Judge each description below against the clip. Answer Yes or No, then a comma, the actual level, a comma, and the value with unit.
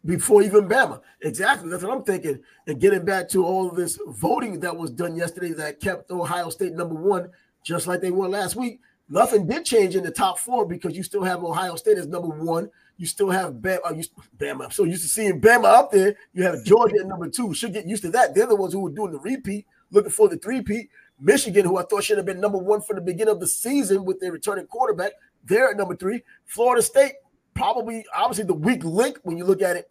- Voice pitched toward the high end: Yes, high, 195 Hz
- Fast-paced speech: Yes, fast, 235 wpm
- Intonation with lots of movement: No, average, 4.3 semitones